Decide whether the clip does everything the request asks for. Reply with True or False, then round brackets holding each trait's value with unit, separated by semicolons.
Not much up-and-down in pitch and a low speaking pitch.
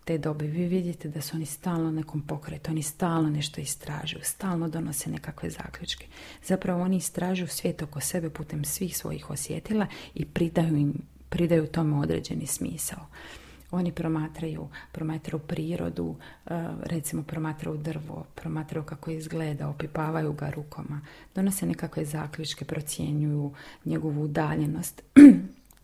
False (1.9 semitones; 160 Hz)